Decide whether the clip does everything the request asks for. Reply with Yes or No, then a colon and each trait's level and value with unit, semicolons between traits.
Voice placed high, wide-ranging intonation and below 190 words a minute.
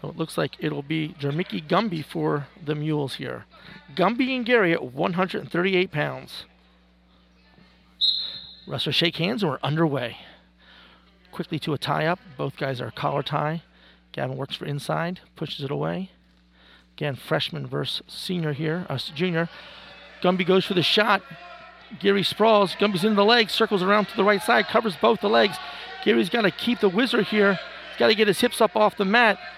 No: medium, 170 Hz; wide, 6.1 semitones; average, 175 wpm